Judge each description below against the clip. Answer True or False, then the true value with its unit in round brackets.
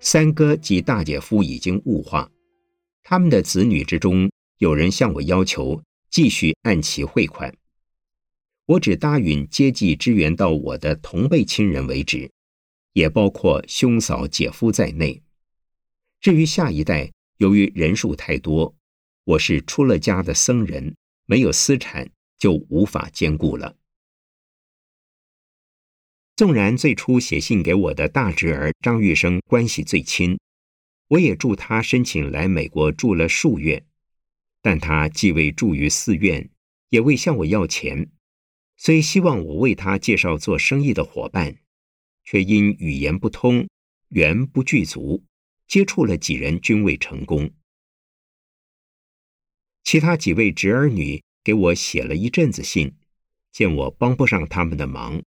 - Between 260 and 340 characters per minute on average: False (205 characters per minute)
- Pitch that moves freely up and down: True (8.6 semitones)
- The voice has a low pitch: True (95 Hz)